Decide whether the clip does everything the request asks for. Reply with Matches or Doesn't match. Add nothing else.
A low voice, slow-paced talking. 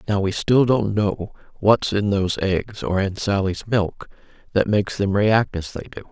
Doesn't match